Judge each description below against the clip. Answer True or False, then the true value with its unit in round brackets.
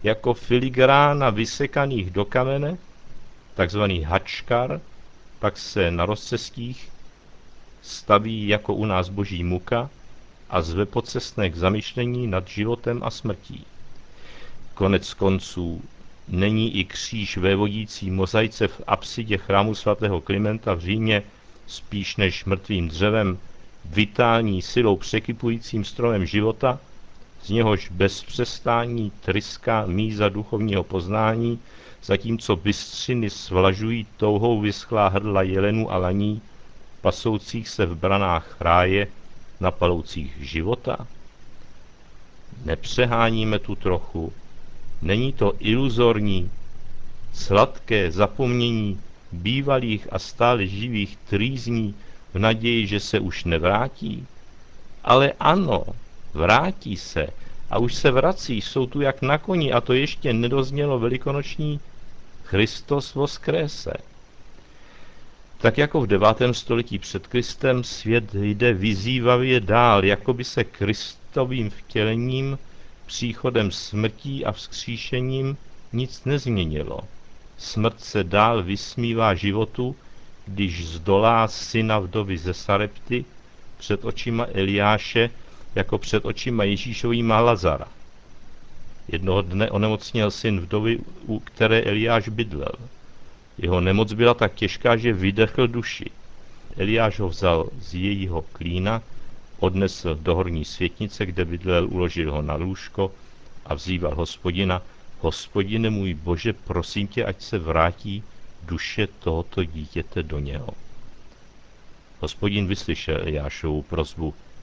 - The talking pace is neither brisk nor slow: False (110 wpm)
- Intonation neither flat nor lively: True (3.7 semitones)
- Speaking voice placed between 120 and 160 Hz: False (105 Hz)